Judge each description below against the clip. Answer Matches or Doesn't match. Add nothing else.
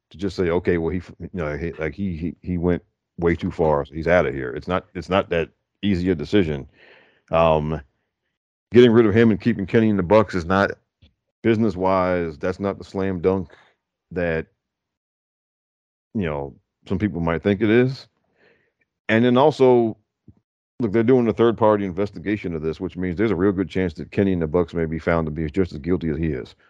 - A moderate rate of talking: Doesn't match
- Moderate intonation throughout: Matches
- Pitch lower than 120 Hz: Matches